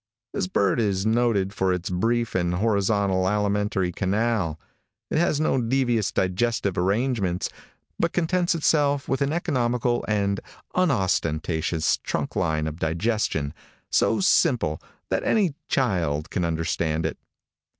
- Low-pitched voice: Yes, low, 100 Hz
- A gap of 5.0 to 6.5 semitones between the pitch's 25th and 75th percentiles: Yes, wide, 5.5 semitones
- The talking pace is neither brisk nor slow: No, slow, 125 wpm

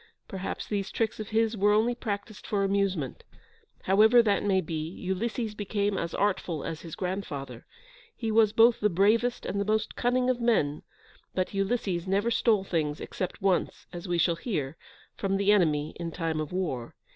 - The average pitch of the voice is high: Yes, high, 195 Hz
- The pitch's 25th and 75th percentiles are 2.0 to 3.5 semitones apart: No, average, 4.0 semitones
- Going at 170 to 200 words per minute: Yes, average, 175 wpm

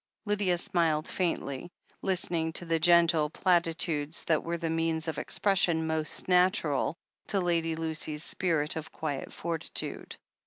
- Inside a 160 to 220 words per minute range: No, average, 140 wpm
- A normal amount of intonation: No, narrow, 1.7 semitones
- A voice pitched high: No, medium, 165 Hz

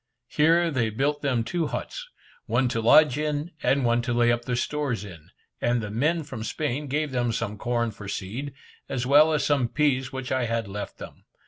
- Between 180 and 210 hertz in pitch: No, low, 130 Hz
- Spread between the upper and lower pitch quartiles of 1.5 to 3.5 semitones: No, average, 4.1 semitones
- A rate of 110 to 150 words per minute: No, fast, 205 wpm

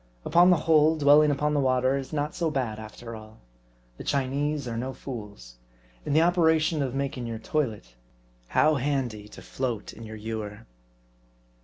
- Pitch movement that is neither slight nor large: Yes, average, 5.0 semitones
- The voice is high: No, low, 135 Hz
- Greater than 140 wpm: Yes, average, 165 wpm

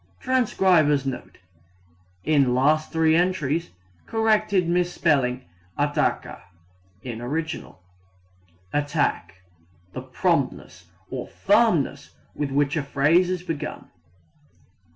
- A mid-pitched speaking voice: Yes, medium, 155 Hz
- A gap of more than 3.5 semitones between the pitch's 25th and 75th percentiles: Yes, average, 4.5 semitones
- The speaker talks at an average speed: No, slow, 90 wpm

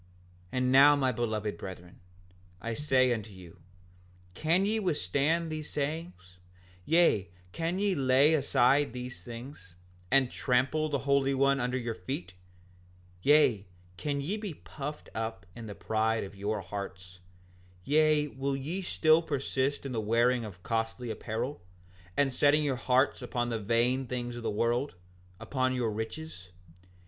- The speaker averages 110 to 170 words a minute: Yes, average, 150 wpm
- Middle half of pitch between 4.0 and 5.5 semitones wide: Yes, average, 4.5 semitones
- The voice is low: Yes, low, 130 Hz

